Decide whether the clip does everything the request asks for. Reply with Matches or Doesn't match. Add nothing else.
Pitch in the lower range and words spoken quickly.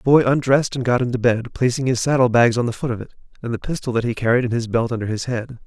Matches